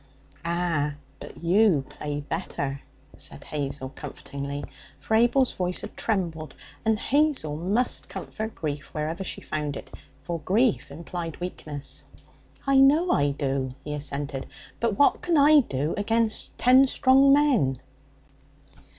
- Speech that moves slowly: Yes, slow, 130 wpm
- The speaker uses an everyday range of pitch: No, wide, 8.2 semitones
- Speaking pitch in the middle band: Yes, medium, 170 Hz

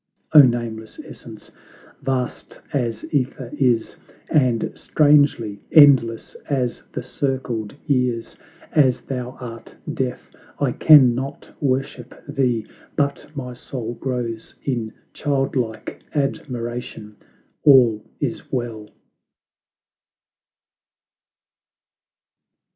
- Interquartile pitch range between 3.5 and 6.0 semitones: No, average, 2.9 semitones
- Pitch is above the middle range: No, low, 125 Hz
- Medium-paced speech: No, slow, 90 wpm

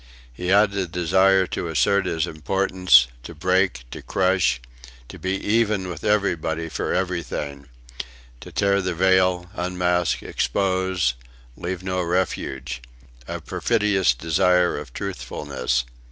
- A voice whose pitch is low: Yes, very low, 90 Hz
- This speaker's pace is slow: Yes, slow, 125 wpm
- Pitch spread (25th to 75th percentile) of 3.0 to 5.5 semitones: No, narrow, 2.4 semitones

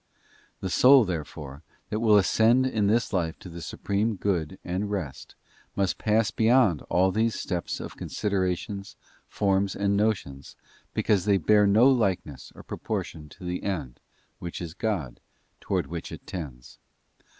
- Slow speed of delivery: No, average, 150 wpm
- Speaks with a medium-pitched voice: No, very low, 95 Hz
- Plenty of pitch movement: No, average, 4.1 semitones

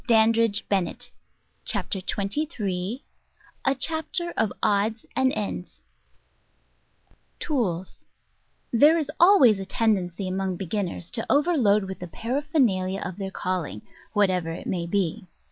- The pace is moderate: No, slow, 130 wpm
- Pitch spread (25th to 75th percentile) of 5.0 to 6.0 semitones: Yes, average, 5.3 semitones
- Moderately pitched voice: No, high, 205 Hz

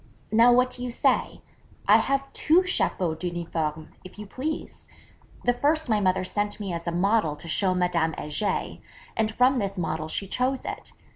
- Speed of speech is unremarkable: Yes, average, 175 wpm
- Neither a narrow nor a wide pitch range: No, wide, 6.4 semitones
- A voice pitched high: Yes, high, 200 Hz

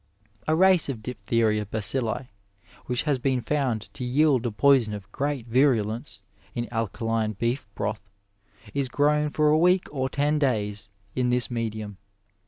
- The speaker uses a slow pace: No, average, 150 wpm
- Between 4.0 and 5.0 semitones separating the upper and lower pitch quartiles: Yes, average, 4.4 semitones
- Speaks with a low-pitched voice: Yes, low, 125 Hz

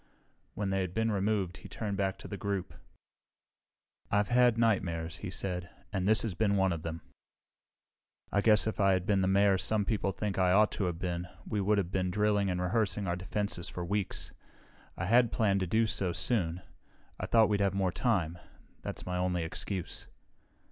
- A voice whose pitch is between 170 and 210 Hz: No, very low, 95 Hz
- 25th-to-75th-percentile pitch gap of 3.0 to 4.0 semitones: No, narrow, 2.6 semitones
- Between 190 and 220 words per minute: Yes, average, 195 wpm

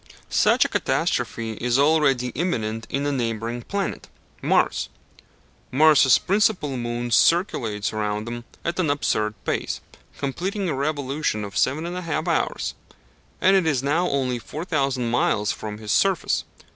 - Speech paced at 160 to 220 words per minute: No, slow, 135 wpm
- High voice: No, low, 135 Hz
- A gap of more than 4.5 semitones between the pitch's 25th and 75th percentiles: Yes, wide, 5.6 semitones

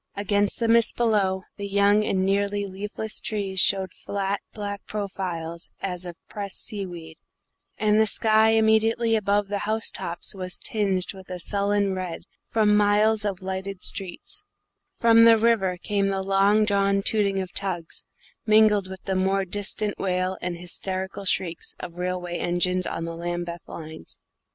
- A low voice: No, high, 195 Hz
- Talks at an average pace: Yes, average, 155 wpm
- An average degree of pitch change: No, narrow, 2.2 semitones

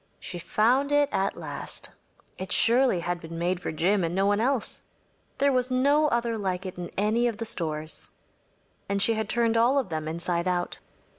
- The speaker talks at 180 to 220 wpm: Yes, average, 195 wpm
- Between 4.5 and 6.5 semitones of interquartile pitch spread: Yes, wide, 5.4 semitones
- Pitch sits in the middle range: No, high, 205 Hz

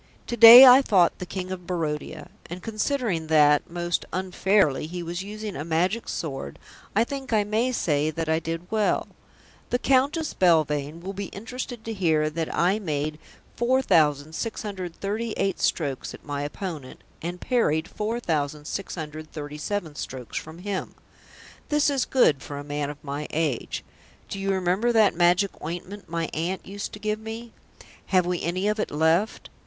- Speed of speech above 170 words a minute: No, average, 155 wpm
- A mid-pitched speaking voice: Yes, medium, 180 Hz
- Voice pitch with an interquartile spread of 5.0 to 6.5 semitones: Yes, average, 5.3 semitones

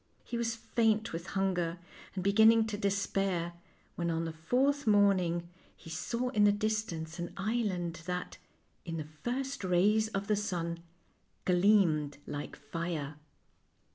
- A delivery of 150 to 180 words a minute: No, average, 140 wpm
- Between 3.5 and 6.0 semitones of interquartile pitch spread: Yes, average, 4.4 semitones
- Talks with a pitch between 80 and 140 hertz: No, high, 195 Hz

